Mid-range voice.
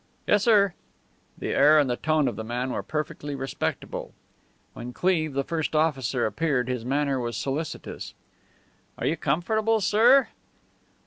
Yes: medium, 150 Hz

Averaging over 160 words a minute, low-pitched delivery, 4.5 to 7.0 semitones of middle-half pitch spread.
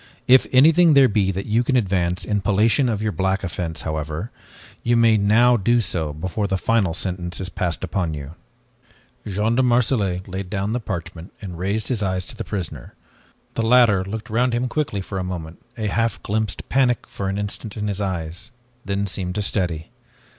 No: average, 190 wpm; low, 100 Hz; average, 3.9 semitones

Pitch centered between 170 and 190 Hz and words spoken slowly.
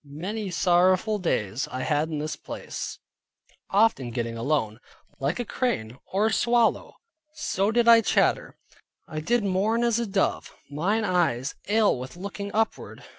No: medium, 185 Hz; average, 150 wpm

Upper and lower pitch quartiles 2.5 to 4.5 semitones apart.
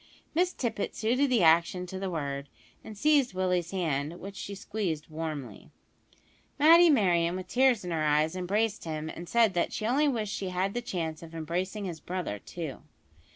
No: average, 5.2 semitones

